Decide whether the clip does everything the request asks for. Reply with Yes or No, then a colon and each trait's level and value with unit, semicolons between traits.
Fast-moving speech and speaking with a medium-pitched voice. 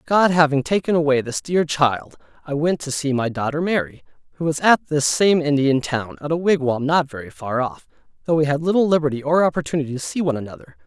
Yes: fast, 215 wpm; medium, 150 Hz